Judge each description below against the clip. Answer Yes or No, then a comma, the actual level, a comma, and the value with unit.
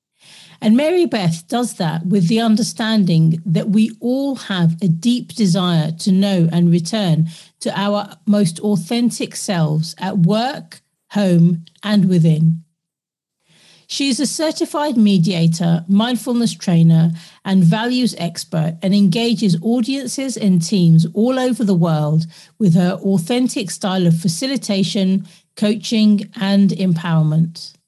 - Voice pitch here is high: Yes, high, 195 Hz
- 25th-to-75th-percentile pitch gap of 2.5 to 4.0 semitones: No, average, 4.8 semitones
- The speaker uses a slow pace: Yes, slow, 125 wpm